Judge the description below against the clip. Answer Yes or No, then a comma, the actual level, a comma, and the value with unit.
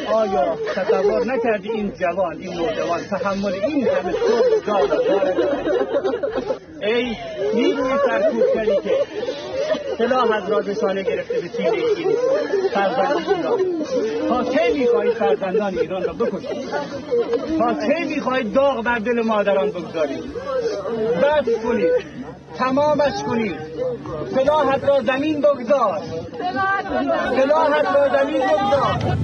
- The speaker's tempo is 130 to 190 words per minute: No, slow, 105 wpm